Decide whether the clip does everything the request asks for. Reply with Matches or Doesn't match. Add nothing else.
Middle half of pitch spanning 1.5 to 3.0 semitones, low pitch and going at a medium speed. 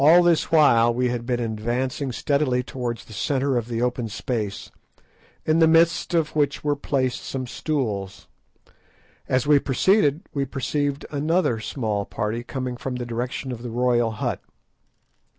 Doesn't match